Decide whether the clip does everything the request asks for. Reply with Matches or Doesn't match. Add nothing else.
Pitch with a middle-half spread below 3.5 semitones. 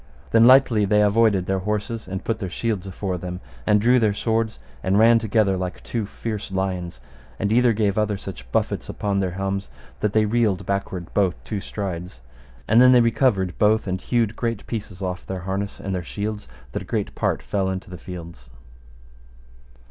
Matches